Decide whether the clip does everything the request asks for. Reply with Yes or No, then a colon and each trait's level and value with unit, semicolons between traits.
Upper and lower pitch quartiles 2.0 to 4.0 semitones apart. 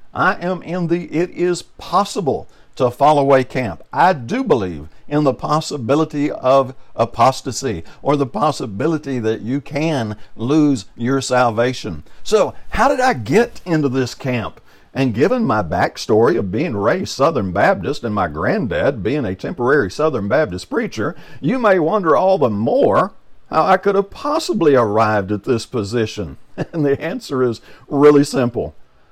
No: average, 5.1 semitones